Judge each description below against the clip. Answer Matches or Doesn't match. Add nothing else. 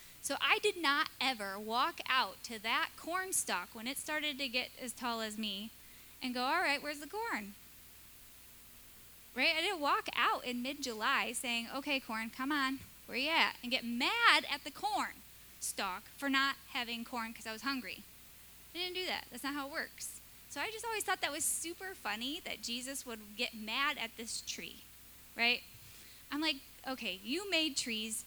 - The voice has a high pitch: Matches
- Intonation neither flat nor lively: Matches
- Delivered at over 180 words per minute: Matches